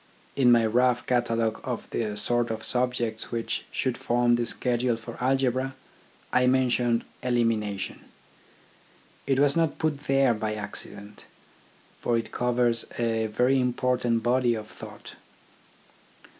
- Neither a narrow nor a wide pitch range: No, narrow, 1.8 semitones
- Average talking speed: No, slow, 130 wpm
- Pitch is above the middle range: No, low, 120 Hz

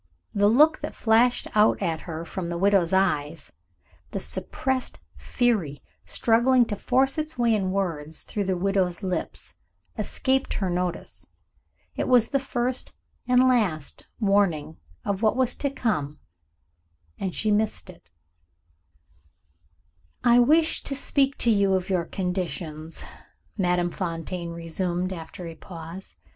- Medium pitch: No, high, 195 Hz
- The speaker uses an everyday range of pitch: No, wide, 5.8 semitones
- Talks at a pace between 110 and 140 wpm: Yes, slow, 135 wpm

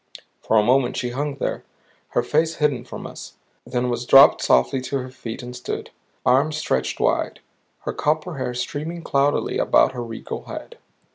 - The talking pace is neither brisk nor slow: Yes, average, 170 wpm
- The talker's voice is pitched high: No, low, 130 Hz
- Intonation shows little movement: No, average, 3.1 semitones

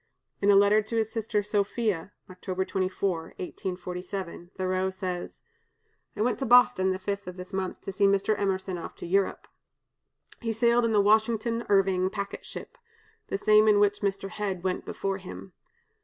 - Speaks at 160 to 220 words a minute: Yes, average, 170 wpm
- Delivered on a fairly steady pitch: Yes, narrow, 2.2 semitones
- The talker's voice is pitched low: No, high, 195 Hz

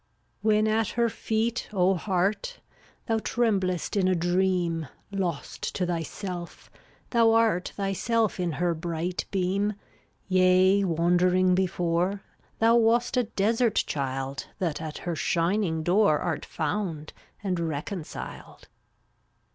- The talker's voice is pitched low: No, medium, 185 Hz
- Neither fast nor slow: No, slow, 120 wpm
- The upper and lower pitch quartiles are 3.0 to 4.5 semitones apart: Yes, average, 3.7 semitones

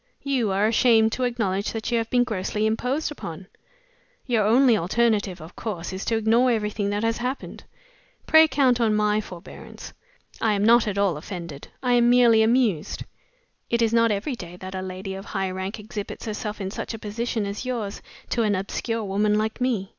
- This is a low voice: No, high, 215 Hz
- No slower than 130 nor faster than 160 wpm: No, average, 190 wpm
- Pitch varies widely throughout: No, average, 3.1 semitones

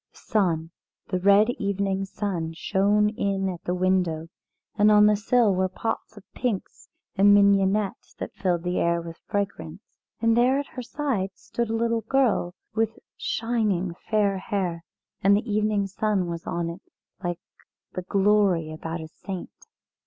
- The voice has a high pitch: Yes, high, 200 Hz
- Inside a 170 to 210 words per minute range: No, average, 160 wpm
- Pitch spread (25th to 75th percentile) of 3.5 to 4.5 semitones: No, average, 3.0 semitones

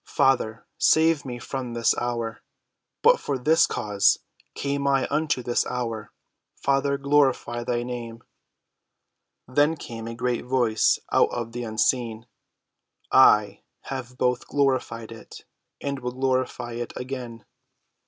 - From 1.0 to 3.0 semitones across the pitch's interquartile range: Yes, average, 2.7 semitones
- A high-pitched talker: No, low, 125 Hz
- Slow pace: Yes, slow, 125 wpm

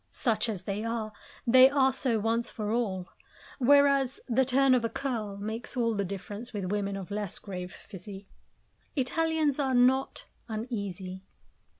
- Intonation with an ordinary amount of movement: Yes, average, 4.3 semitones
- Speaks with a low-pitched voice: No, high, 230 Hz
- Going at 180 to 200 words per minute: No, average, 155 wpm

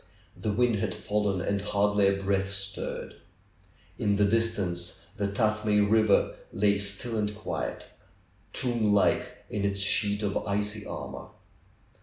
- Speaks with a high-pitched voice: No, low, 105 Hz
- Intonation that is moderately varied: No, narrow, 1.1 semitones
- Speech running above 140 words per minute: No, slow, 135 wpm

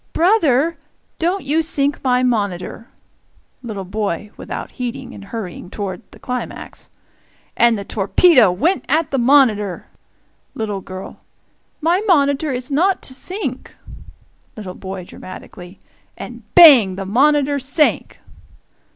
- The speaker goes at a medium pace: No, slow, 120 wpm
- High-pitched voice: Yes, very high, 250 Hz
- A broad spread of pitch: Yes, wide, 6.7 semitones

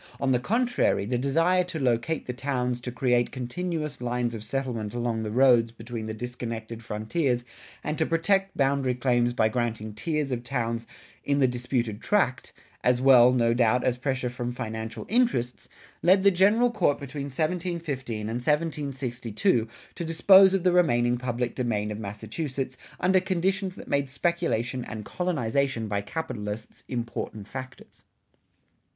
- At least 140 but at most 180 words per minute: Yes, average, 150 wpm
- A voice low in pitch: Yes, low, 125 Hz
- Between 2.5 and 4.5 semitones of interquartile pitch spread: No, average, 5.2 semitones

